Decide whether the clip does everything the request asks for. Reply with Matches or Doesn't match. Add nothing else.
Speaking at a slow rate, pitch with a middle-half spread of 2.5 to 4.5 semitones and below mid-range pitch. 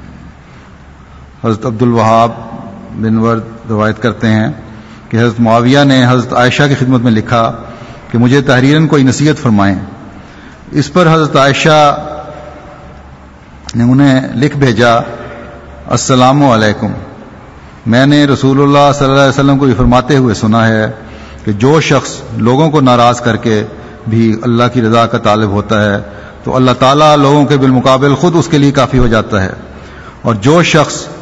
Doesn't match